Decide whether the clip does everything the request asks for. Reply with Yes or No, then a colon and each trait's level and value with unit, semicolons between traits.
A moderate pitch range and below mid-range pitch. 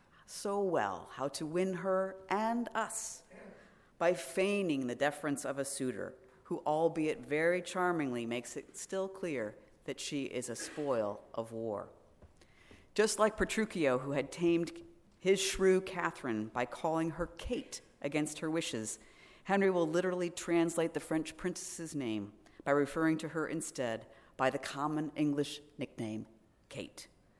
No: average, 4.9 semitones; medium, 165 Hz